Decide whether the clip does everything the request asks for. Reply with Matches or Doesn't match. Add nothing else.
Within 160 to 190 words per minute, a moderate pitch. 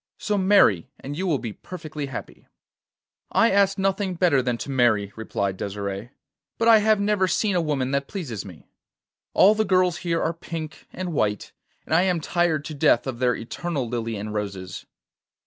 Matches